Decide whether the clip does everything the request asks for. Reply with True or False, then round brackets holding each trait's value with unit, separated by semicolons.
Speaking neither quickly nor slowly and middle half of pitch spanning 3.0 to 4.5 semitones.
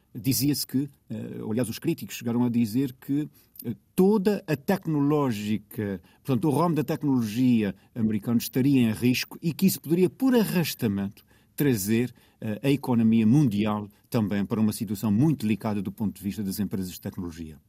False (155 wpm; 5.3 semitones)